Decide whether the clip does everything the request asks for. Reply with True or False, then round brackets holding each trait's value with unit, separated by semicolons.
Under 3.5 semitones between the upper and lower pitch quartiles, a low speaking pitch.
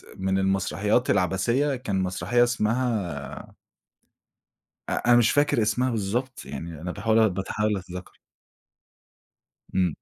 False (4.4 semitones; 105 Hz)